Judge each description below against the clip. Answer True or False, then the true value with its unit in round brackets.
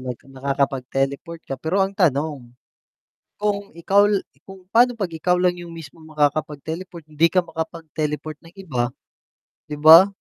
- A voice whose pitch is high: False (160 Hz)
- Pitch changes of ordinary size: True (4.0 semitones)